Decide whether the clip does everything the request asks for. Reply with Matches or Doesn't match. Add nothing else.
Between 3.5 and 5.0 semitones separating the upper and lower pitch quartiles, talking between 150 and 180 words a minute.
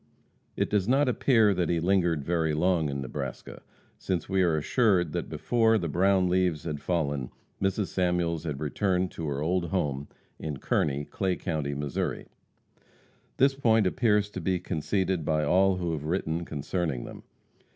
Matches